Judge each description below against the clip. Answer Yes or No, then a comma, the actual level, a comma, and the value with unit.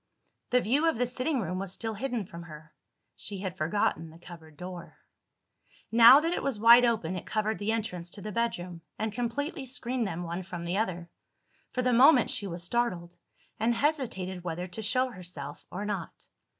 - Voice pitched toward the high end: Yes, high, 205 Hz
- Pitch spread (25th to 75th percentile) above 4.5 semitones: Yes, wide, 5.5 semitones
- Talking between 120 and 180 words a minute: No, average, 190 wpm